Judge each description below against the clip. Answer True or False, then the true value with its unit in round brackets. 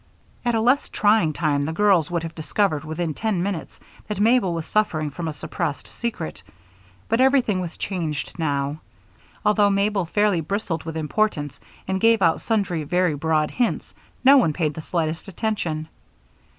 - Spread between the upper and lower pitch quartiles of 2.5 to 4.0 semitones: False (5.0 semitones)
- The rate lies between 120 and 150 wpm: False (165 wpm)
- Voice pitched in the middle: True (175 Hz)